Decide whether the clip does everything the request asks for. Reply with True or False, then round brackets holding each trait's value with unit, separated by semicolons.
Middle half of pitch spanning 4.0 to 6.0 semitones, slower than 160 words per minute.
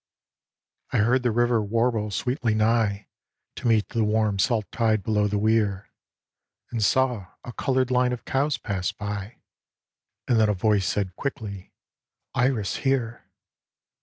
False (2.9 semitones; 150 wpm)